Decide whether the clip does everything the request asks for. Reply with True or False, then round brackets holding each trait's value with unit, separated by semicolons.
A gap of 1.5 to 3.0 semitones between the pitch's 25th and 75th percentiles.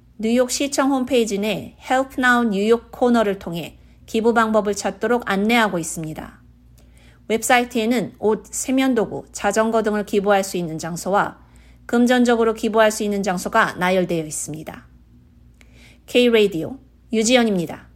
False (5.2 semitones)